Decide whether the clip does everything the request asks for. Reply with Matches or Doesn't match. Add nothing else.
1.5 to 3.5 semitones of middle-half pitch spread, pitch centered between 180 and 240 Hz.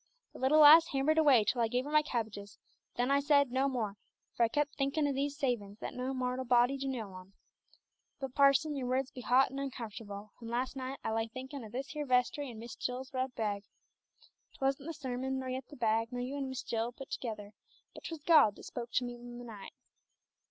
Doesn't match